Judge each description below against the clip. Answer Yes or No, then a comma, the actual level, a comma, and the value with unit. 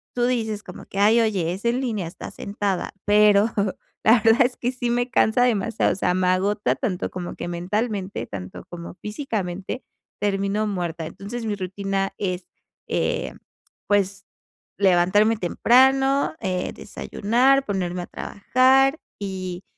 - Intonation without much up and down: No, average, 4.2 semitones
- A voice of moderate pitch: No, high, 205 Hz